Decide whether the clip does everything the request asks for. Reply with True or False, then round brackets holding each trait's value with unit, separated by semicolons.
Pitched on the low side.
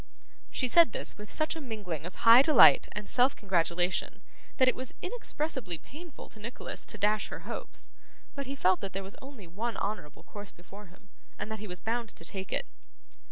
False (215 Hz)